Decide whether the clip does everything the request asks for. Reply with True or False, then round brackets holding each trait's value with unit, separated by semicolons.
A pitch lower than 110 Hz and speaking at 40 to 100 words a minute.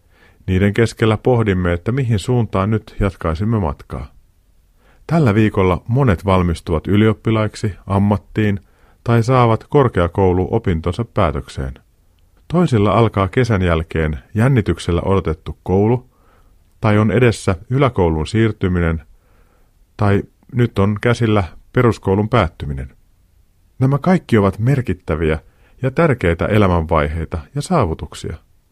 True (95 Hz; 95 wpm)